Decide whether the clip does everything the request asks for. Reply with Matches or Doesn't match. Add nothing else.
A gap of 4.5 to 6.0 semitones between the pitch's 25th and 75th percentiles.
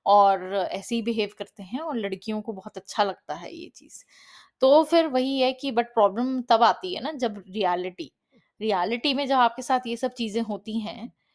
Doesn't match